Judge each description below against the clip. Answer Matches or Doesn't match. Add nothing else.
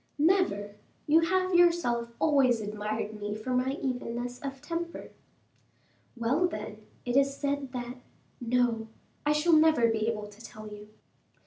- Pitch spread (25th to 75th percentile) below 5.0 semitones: Doesn't match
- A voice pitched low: Doesn't match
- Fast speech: Doesn't match